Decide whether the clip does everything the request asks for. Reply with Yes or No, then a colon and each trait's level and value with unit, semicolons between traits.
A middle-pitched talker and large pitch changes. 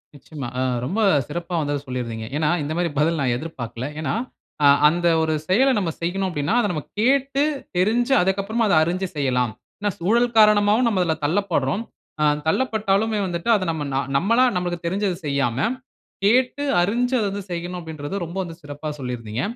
Yes: medium, 175 Hz; wide, 6.3 semitones